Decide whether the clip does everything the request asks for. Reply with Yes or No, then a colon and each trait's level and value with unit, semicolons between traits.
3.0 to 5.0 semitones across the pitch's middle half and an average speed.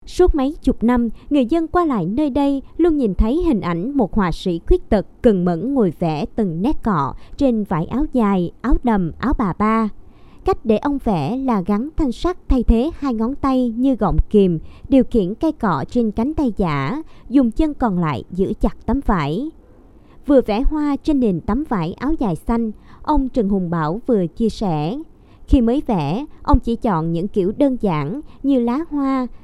No: wide, 5.5 semitones; average, 200 wpm